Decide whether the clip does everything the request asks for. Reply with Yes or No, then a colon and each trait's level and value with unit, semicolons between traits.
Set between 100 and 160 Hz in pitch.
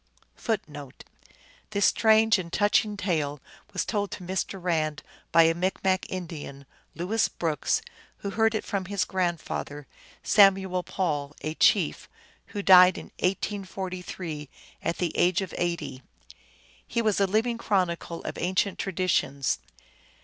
No: medium, 185 Hz